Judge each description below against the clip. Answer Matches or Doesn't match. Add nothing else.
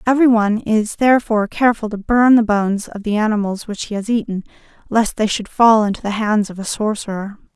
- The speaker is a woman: Matches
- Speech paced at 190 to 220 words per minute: Matches